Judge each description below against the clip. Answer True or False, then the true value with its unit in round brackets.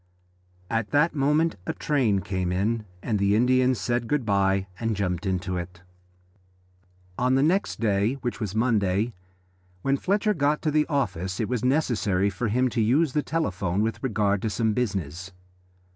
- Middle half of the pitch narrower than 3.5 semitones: False (5.1 semitones)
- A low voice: True (115 Hz)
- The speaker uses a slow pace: False (165 wpm)